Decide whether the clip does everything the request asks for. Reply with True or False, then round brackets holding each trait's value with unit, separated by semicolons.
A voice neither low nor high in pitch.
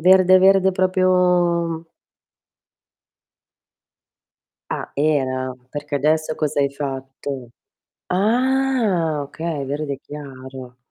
True (155 Hz)